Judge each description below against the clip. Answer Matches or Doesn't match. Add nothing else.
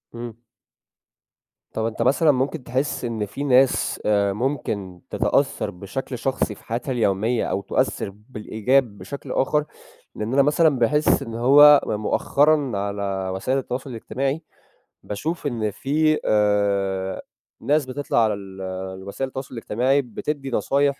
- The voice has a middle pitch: Doesn't match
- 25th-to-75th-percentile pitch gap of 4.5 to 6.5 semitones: Matches